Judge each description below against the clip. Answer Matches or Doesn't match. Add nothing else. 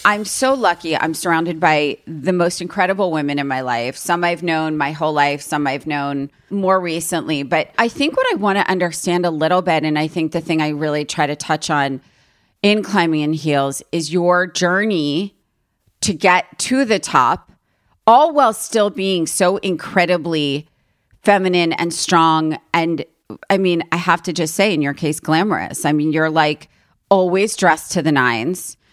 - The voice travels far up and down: Doesn't match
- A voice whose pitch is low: Doesn't match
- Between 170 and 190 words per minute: Matches